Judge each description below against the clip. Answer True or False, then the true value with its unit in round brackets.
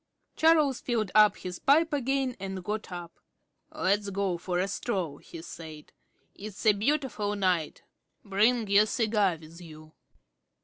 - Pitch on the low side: False (200 Hz)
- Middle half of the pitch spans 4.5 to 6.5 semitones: True (4.8 semitones)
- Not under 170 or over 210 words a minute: False (135 wpm)